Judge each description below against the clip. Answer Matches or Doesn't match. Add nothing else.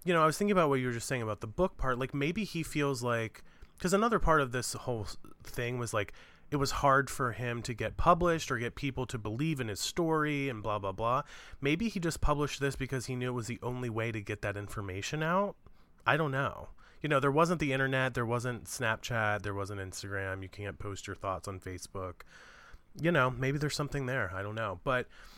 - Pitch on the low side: Matches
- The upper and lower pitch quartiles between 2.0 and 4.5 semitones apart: Doesn't match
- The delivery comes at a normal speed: Doesn't match